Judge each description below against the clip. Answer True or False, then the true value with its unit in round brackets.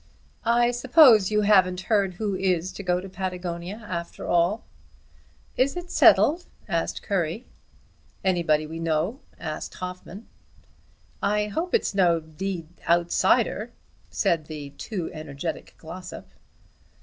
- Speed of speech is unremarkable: False (120 wpm)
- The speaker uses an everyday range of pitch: True (3.9 semitones)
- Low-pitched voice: False (185 Hz)